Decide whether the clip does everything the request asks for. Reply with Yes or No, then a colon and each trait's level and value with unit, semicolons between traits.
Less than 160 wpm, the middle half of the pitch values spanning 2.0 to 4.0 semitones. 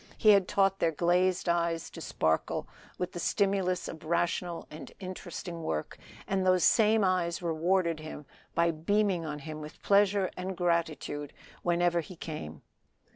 Yes: average, 150 wpm; narrow, 2.4 semitones